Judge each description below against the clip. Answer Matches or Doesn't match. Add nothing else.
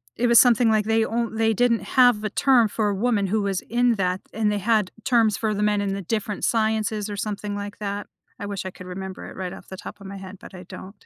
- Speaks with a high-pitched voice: Matches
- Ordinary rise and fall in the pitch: Doesn't match